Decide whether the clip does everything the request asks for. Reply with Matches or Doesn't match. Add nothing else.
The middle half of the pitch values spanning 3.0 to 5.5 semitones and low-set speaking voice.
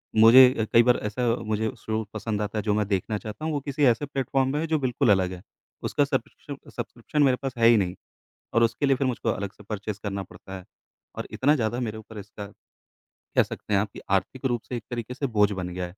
Matches